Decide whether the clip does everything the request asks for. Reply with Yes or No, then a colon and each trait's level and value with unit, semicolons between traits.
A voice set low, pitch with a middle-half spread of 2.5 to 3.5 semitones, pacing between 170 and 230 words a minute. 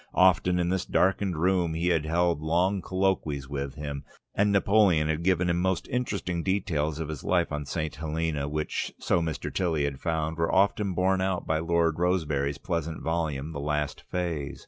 Yes: very low, 85 Hz; average, 3.1 semitones; average, 180 wpm